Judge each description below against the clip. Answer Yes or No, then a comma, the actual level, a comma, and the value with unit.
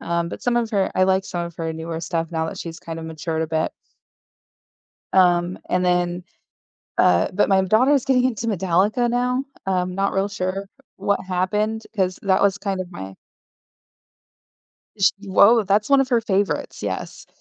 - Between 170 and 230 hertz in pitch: Yes, high, 190 Hz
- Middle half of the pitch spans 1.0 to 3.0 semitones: No, average, 3.4 semitones